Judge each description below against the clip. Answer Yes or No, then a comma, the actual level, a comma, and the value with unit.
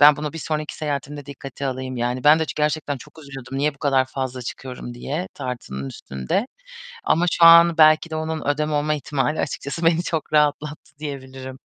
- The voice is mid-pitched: Yes, medium, 145 Hz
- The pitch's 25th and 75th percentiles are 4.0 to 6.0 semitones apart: No, average, 2.8 semitones